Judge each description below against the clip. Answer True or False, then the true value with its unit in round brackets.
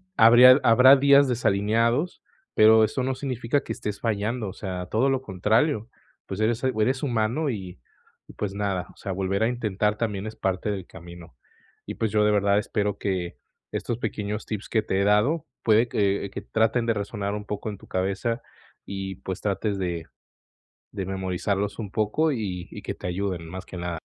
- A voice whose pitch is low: True (105 Hz)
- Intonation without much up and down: False (3.1 semitones)